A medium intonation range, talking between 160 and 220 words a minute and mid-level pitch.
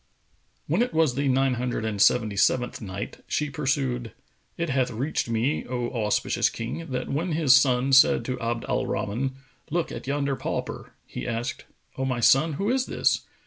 No: average, 3.3 semitones; average, 180 wpm; low, 130 Hz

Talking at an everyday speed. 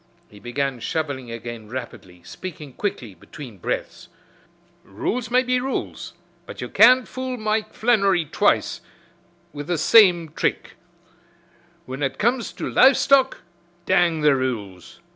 No: slow, 130 wpm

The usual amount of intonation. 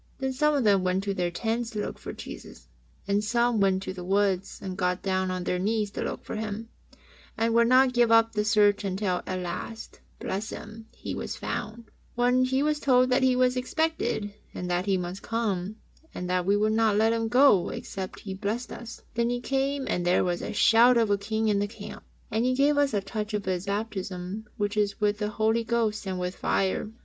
Yes: average, 3.4 semitones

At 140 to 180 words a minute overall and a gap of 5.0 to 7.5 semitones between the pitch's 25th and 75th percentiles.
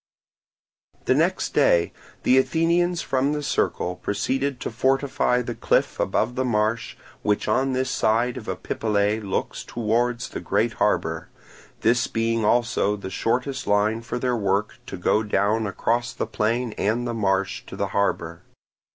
No: average, 150 wpm; average, 3.4 semitones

